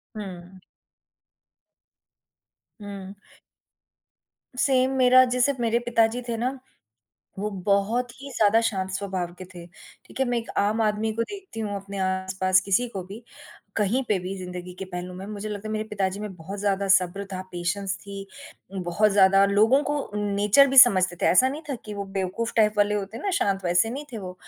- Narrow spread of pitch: No, average, 3.3 semitones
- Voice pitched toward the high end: Yes, high, 205 Hz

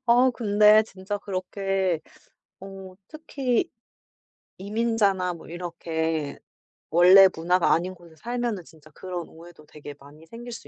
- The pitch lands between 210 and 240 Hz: No, medium, 185 Hz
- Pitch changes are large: No, average, 4.2 semitones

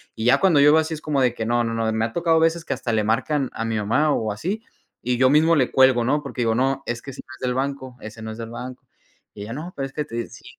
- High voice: No, low, 130 Hz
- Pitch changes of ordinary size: Yes, average, 4.4 semitones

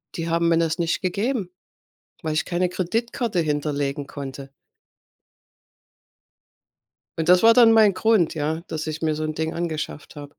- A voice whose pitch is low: No, medium, 165 Hz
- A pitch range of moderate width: Yes, average, 3.2 semitones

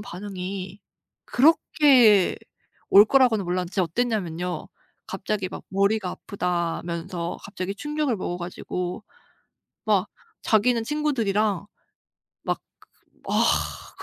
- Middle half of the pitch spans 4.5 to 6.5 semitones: No, average, 3.8 semitones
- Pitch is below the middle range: No, high, 200 Hz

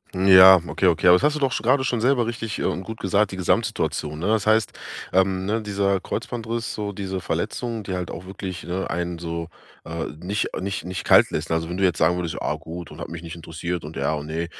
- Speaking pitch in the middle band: No, very low, 95 Hz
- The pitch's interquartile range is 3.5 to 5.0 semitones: Yes, average, 3.8 semitones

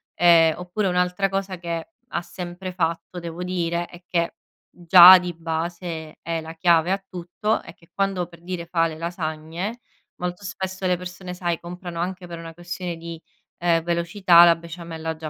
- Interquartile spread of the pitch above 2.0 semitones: No, narrow, 1.4 semitones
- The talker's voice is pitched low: No, medium, 175 Hz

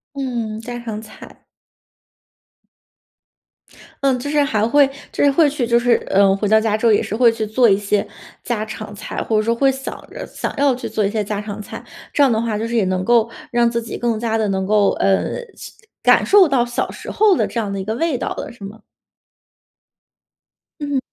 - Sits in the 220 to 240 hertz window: Yes, high, 230 Hz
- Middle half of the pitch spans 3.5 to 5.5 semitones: No, average, 2.9 semitones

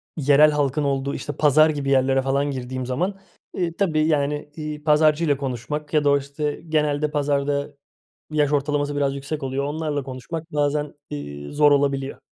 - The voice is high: No, medium, 145 Hz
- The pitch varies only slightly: Yes, narrow, 1.6 semitones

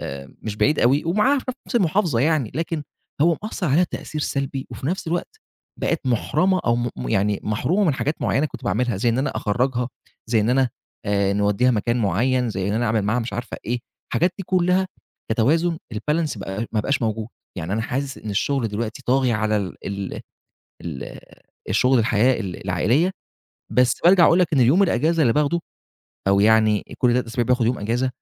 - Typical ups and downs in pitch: No, wide, 6.1 semitones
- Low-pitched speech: Yes, low, 125 Hz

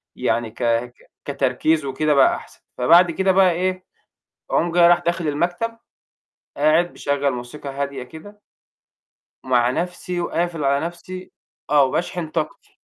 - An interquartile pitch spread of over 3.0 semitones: Yes, average, 4.2 semitones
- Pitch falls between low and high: Yes, medium, 160 Hz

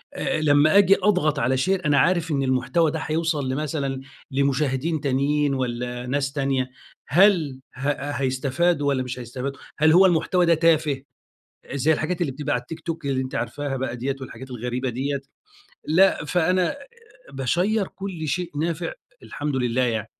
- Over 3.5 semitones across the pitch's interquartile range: Yes, average, 3.9 semitones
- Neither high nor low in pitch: Yes, medium, 145 Hz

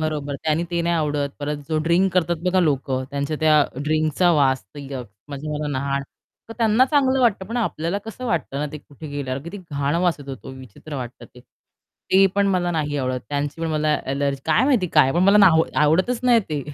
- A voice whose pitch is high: No, medium, 155 Hz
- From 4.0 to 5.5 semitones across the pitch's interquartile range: Yes, average, 4.5 semitones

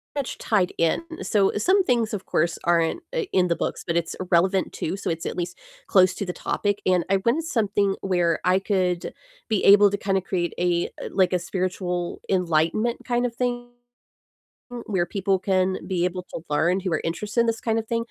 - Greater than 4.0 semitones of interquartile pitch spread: No, average, 3.3 semitones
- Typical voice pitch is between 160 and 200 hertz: Yes, high, 190 Hz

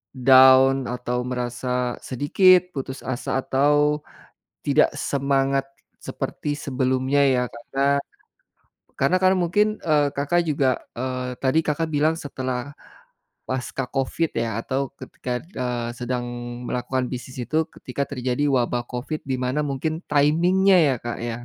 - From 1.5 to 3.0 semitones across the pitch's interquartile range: Yes, average, 2.7 semitones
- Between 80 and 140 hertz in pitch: Yes, low, 135 Hz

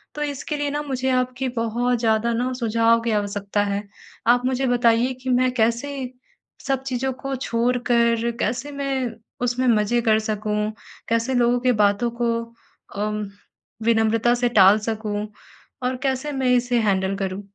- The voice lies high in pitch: Yes, high, 235 Hz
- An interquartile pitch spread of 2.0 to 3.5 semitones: Yes, average, 2.7 semitones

